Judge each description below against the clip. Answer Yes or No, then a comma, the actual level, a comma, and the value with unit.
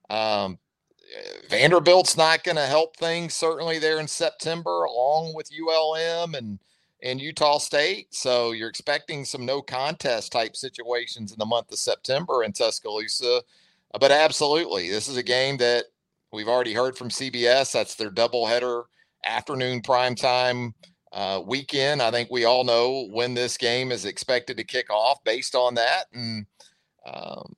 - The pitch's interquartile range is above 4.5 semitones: Yes, average, 4.9 semitones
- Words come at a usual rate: Yes, average, 150 wpm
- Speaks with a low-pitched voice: Yes, low, 130 Hz